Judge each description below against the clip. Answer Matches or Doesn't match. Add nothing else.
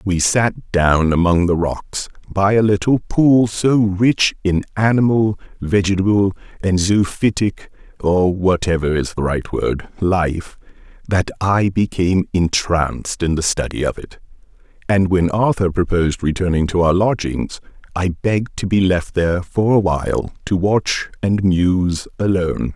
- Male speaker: Matches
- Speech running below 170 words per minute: Matches